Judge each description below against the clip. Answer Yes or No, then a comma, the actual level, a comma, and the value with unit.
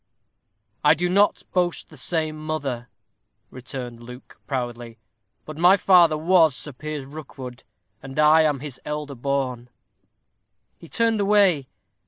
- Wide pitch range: No, average, 4.2 semitones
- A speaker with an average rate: No, slow, 130 wpm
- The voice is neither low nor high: Yes, medium, 150 Hz